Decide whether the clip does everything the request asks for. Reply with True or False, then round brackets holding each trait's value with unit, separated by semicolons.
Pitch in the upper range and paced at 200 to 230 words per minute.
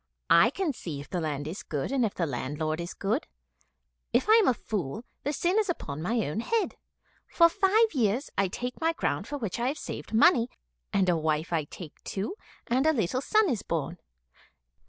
True (220 Hz; 205 wpm)